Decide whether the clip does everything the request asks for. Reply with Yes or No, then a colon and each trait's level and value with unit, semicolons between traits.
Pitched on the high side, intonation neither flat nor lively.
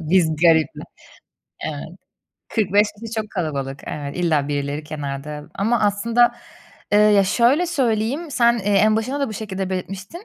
No: high, 200 Hz; wide, 6.6 semitones